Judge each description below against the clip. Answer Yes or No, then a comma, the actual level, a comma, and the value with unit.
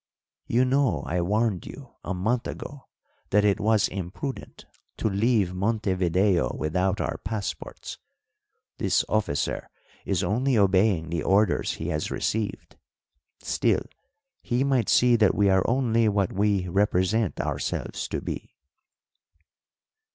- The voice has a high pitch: No, low, 100 Hz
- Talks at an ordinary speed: No, slow, 125 wpm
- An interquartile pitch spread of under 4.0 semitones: Yes, average, 3.4 semitones